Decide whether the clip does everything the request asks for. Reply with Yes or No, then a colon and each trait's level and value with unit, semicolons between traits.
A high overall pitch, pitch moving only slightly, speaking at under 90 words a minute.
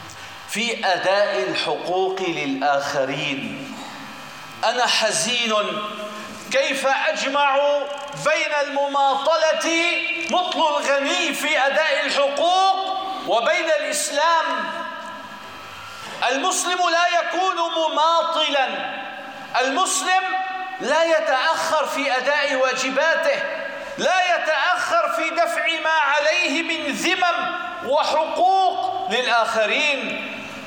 No: very high, 305 Hz; average, 3.7 semitones; average, 70 wpm